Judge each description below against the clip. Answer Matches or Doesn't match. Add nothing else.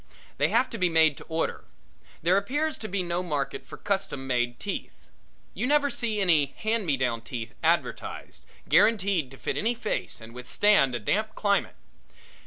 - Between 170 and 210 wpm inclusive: Matches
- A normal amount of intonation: Doesn't match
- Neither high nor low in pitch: Matches